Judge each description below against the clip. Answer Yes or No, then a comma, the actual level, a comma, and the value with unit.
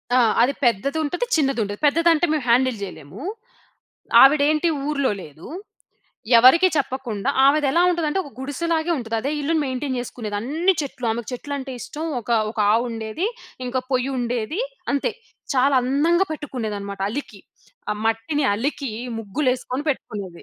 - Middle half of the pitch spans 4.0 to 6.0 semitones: Yes, average, 4.5 semitones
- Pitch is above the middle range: Yes, very high, 265 Hz